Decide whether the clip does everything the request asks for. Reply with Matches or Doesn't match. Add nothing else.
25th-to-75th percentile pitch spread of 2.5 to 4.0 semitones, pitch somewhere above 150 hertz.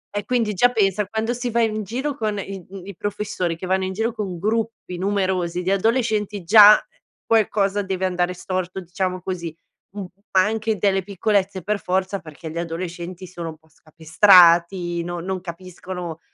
Matches